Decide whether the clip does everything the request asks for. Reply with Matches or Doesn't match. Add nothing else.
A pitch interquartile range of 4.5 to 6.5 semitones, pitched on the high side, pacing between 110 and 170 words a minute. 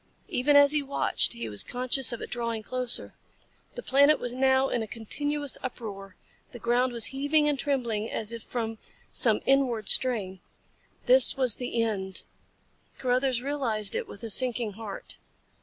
Doesn't match